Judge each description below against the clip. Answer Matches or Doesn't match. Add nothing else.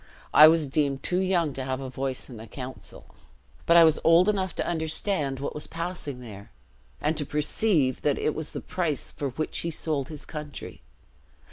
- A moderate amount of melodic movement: Matches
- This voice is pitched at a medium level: Matches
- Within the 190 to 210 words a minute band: Matches